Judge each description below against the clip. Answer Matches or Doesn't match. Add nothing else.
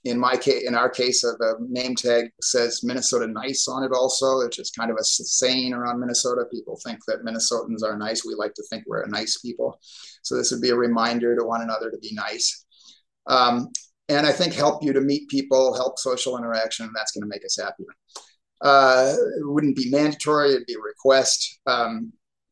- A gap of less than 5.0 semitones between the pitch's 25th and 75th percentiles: Matches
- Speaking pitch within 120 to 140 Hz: Matches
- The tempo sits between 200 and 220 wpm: Matches